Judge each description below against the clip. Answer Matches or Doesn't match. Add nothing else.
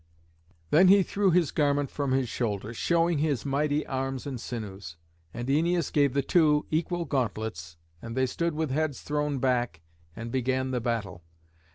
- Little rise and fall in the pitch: Doesn't match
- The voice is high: Doesn't match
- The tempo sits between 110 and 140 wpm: Doesn't match